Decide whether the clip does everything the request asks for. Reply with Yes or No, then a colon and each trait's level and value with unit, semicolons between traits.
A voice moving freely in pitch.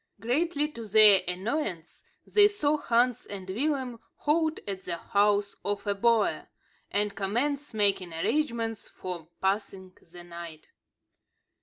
Yes: wide, 6.0 semitones